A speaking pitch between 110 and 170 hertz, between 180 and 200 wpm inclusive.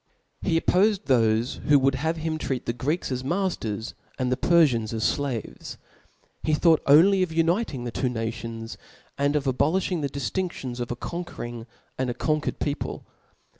Yes: medium, 140 Hz; average, 195 wpm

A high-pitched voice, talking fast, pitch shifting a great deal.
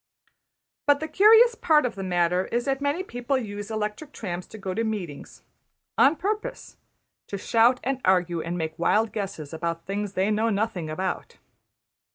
No: high, 210 Hz; average, 170 wpm; wide, 6.8 semitones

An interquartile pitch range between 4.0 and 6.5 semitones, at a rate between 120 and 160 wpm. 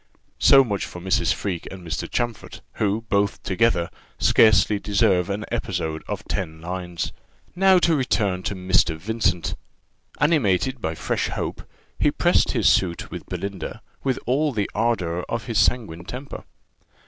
Yes: average, 4.7 semitones; average, 150 wpm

